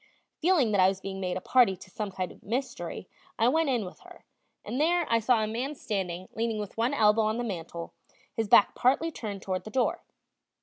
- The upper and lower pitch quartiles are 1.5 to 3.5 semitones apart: No, average, 4.8 semitones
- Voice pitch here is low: No, high, 220 Hz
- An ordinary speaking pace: No, fast, 220 wpm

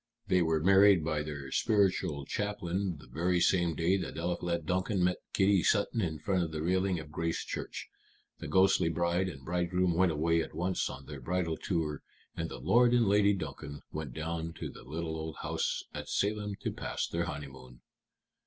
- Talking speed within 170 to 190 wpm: Yes, average, 180 wpm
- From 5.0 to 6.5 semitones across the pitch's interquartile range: No, average, 3.2 semitones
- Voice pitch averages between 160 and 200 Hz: No, very low, 85 Hz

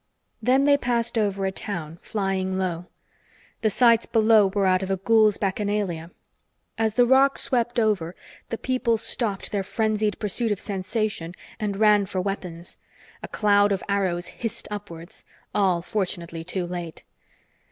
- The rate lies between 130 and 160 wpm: Yes, average, 150 wpm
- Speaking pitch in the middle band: No, high, 205 Hz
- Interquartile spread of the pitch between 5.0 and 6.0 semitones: No, average, 3.1 semitones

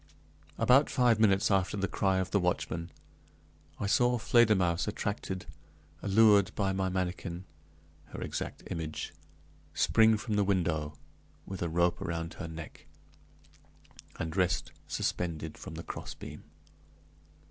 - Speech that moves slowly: Yes, slow, 125 wpm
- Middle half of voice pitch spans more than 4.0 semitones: No, average, 3.4 semitones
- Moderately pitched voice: No, very low, 95 Hz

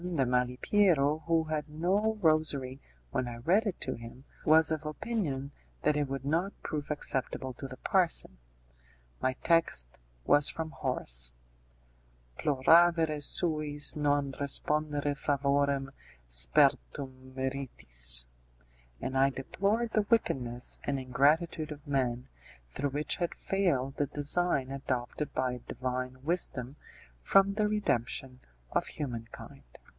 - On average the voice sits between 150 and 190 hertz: No, medium, 140 Hz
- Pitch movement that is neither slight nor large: Yes, average, 3.7 semitones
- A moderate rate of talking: No, slow, 120 wpm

